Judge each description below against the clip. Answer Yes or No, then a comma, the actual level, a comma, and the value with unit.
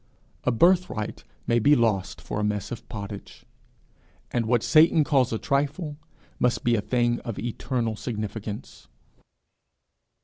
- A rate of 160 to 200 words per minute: No, slow, 135 wpm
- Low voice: Yes, low, 120 Hz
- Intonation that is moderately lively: Yes, average, 4.3 semitones